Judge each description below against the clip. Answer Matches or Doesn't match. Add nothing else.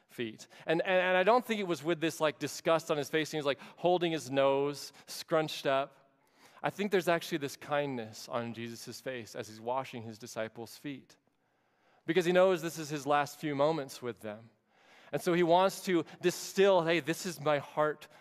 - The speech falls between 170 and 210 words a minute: Matches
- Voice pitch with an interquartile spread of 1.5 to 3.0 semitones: Doesn't match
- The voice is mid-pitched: Matches